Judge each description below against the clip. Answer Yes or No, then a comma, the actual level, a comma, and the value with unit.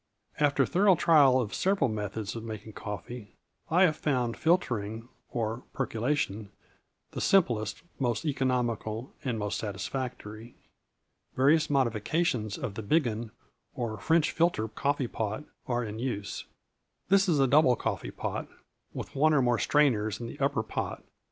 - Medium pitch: No, low, 120 Hz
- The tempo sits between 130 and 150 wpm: Yes, average, 140 wpm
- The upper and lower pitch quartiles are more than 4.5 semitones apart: Yes, average, 5.2 semitones